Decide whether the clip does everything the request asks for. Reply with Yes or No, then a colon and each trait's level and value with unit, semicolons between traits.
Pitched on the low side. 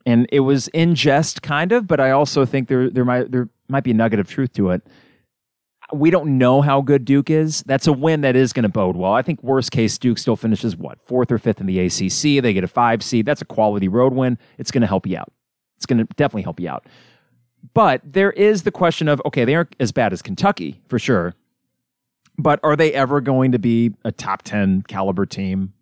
Yes: low, 130 Hz